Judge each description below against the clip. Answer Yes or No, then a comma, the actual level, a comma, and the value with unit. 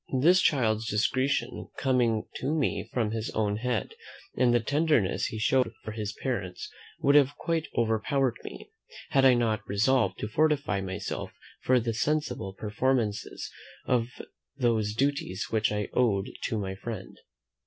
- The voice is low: Yes, low, 115 Hz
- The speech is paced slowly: No, average, 150 wpm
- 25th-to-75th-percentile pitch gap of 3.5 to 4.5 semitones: Yes, average, 4.1 semitones